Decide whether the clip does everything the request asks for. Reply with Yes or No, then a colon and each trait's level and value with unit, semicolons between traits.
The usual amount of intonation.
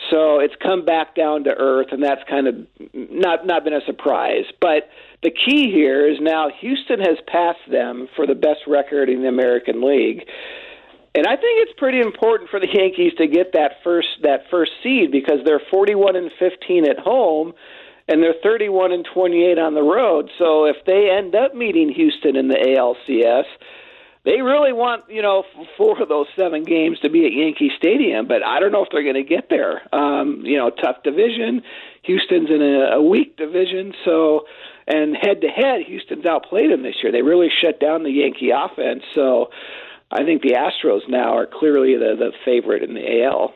No: wide, 8.7 semitones